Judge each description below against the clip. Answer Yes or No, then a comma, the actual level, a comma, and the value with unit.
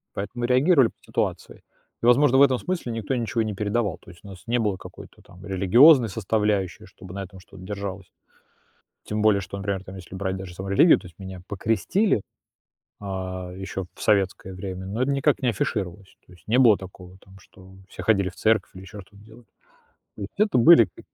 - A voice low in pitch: Yes, low, 100 Hz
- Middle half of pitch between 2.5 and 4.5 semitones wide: Yes, average, 3.6 semitones